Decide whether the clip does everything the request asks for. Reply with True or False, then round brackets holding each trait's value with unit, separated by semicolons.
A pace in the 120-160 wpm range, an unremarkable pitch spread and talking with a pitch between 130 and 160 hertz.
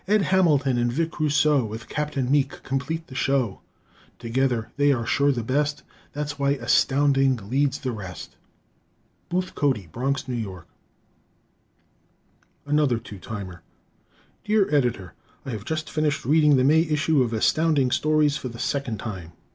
True (145 wpm; 4.0 semitones; 135 Hz)